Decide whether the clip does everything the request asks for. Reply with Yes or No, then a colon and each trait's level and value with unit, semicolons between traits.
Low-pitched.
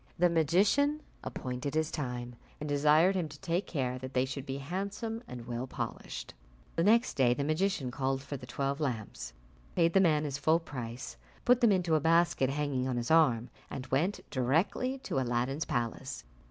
No: medium, 145 Hz